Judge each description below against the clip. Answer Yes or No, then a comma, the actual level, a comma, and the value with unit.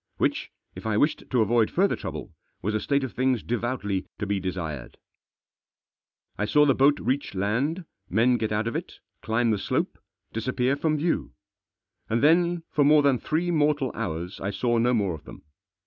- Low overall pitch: Yes, low, 120 Hz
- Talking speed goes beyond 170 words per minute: Yes, average, 180 wpm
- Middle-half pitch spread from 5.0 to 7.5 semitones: Yes, wide, 5.4 semitones